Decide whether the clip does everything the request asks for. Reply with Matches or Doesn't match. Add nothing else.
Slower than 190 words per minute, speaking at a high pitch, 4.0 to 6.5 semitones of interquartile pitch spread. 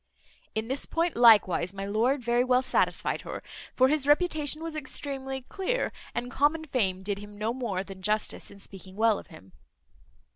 Matches